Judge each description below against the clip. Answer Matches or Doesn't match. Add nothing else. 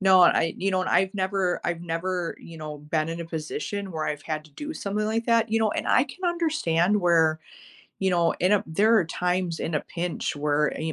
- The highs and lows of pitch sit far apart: Doesn't match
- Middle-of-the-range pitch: Matches